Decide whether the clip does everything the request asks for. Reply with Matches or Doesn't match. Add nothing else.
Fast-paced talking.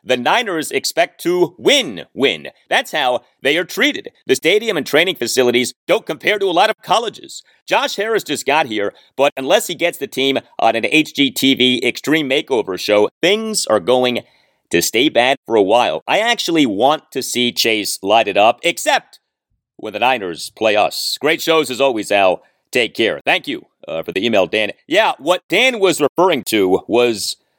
Doesn't match